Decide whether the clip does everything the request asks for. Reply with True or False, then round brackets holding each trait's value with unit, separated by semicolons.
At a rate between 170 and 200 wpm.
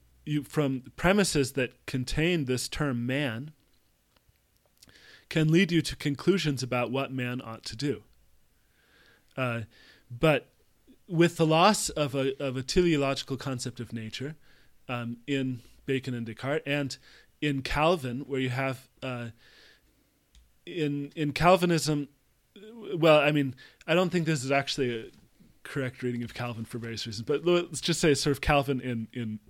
False (150 wpm)